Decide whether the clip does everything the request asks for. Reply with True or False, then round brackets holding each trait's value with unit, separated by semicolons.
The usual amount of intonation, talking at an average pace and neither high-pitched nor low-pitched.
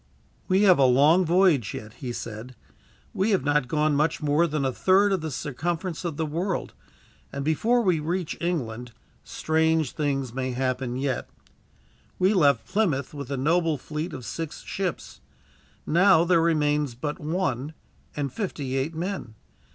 True (4.6 semitones; 160 wpm; 150 Hz)